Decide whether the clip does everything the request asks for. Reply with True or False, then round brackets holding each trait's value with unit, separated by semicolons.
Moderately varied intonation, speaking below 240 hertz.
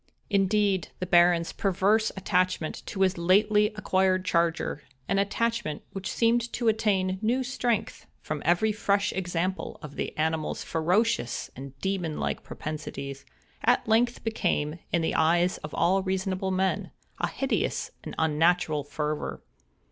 True (4.5 semitones; 185 Hz)